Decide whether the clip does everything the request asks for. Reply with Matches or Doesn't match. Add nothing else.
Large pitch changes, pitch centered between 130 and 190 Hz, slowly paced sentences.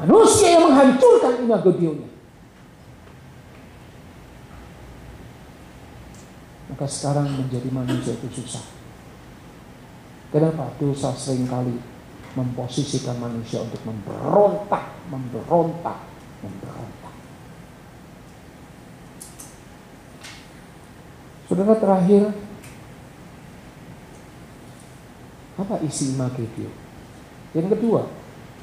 Matches